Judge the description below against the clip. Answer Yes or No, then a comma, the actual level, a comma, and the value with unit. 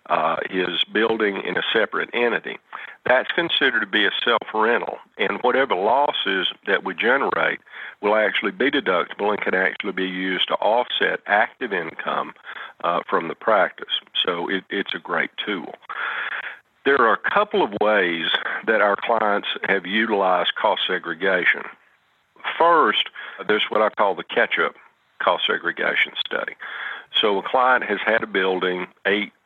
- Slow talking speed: No, average, 150 wpm